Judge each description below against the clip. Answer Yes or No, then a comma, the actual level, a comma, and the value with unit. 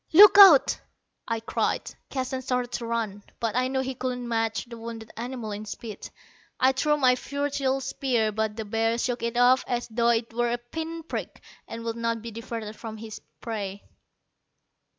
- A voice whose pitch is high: Yes, high, 235 Hz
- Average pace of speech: Yes, average, 185 wpm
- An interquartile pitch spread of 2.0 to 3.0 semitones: Yes, narrow, 2.4 semitones